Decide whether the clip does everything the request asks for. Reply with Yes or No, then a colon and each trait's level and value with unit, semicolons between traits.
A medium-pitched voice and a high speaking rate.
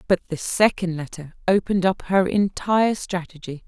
No: medium, 180 Hz; average, 145 wpm